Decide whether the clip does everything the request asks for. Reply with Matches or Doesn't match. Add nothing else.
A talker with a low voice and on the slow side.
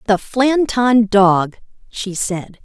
Doesn't match